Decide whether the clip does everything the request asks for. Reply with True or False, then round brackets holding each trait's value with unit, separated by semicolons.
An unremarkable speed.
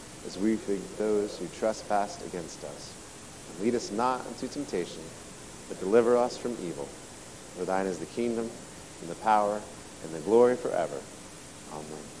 True (155 wpm)